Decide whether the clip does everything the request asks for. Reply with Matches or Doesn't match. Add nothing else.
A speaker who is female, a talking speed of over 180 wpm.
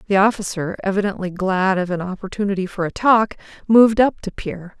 Doesn't match